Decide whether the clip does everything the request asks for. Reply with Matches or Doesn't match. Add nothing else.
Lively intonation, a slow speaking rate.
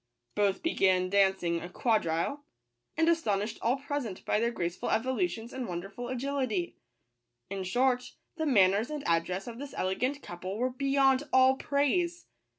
Doesn't match